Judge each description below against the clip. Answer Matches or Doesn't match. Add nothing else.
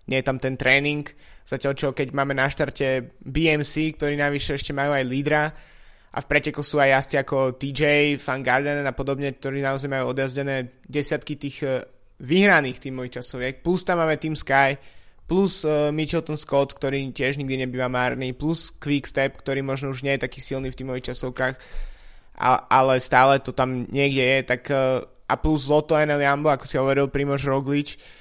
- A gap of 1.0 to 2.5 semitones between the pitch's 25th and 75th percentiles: Matches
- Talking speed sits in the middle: Doesn't match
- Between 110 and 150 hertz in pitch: Matches